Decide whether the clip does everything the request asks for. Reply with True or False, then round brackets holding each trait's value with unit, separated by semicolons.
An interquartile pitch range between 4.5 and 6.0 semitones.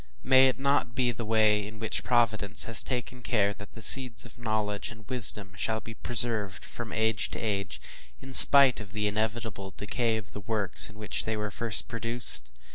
False (2.4 semitones)